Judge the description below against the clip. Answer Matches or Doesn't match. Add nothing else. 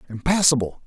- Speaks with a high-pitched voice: Doesn't match